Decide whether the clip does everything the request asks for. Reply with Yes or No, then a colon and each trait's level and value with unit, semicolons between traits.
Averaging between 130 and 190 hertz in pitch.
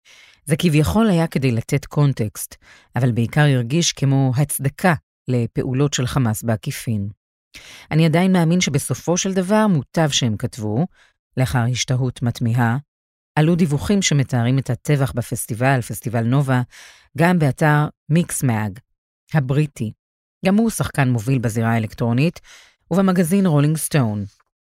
Yes: low, 135 Hz